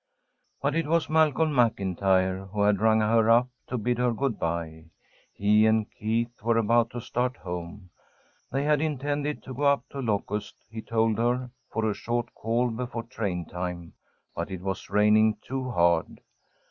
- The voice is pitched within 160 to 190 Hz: No, low, 115 Hz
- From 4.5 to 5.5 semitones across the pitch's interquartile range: No, average, 3.9 semitones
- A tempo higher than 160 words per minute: Yes, average, 170 wpm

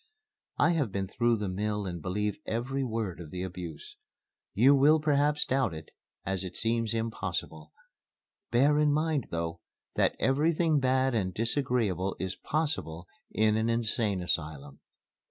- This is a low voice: Yes, low, 110 Hz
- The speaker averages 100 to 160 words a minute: Yes, average, 145 wpm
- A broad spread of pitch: Yes, wide, 6.6 semitones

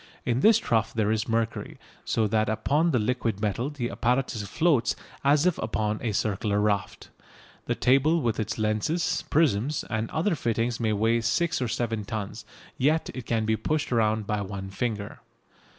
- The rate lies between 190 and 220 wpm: No, average, 170 wpm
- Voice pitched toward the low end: Yes, low, 115 Hz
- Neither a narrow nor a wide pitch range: Yes, average, 3.9 semitones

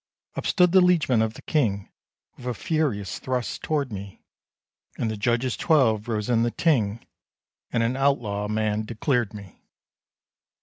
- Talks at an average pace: Yes, average, 160 wpm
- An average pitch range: Yes, average, 4.4 semitones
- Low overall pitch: Yes, low, 115 Hz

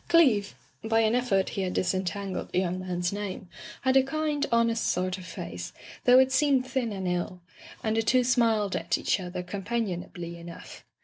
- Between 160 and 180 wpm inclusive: No, average, 195 wpm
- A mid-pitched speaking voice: No, high, 205 Hz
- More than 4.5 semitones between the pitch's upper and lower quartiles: Yes, average, 5.1 semitones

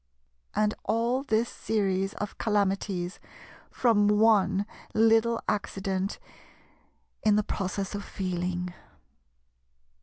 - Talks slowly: Yes, slow, 90 wpm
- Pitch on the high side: Yes, high, 205 Hz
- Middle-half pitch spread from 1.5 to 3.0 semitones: Yes, narrow, 2.4 semitones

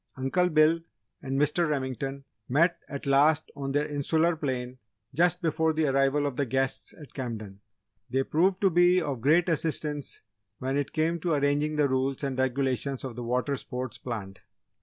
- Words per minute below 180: Yes, average, 170 wpm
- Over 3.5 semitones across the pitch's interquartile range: No, average, 3.2 semitones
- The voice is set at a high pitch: No, medium, 140 Hz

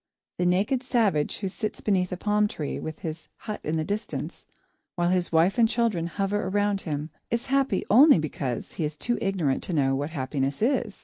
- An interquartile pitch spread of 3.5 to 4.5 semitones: No, average, 5.2 semitones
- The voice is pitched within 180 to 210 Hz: Yes, medium, 185 Hz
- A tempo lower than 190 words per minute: No, average, 195 wpm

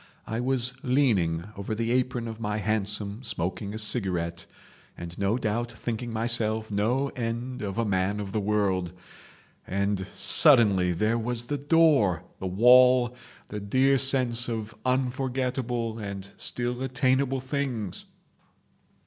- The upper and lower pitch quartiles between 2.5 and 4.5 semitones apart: Yes, average, 3.8 semitones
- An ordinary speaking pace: No, slow, 130 wpm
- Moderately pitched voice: No, low, 115 Hz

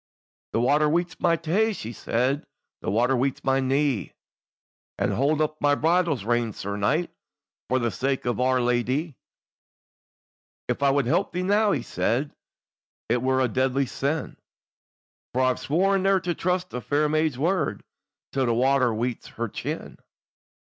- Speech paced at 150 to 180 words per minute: Yes, average, 160 wpm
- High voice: No, low, 135 Hz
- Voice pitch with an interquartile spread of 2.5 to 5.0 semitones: Yes, average, 4.4 semitones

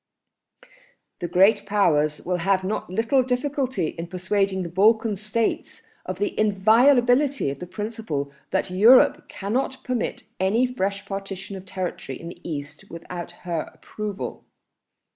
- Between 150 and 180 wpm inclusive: No, slow, 135 wpm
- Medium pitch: No, high, 195 Hz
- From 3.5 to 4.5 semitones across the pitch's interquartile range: Yes, average, 4.2 semitones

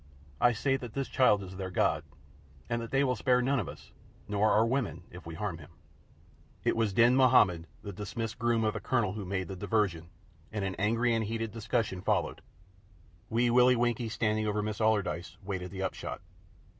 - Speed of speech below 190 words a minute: No, average, 195 wpm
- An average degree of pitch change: Yes, average, 3.4 semitones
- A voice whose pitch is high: No, low, 110 Hz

